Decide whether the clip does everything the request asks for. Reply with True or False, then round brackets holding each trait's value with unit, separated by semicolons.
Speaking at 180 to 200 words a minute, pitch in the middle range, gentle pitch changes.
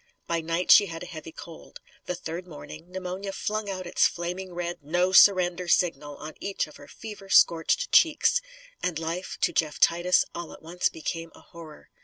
True (185 wpm; 175 Hz; 2.2 semitones)